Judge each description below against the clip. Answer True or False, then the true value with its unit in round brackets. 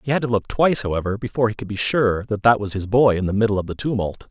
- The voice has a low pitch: True (110 Hz)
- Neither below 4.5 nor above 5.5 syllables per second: False (7.0 syllables/s)